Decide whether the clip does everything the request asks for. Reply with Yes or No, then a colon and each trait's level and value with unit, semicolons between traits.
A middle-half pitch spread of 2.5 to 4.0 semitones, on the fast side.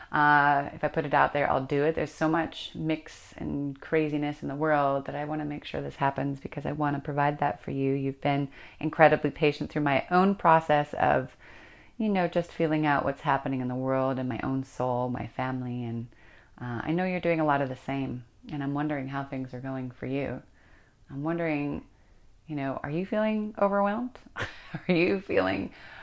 Yes: average, 3.0 semitones; fast, 210 wpm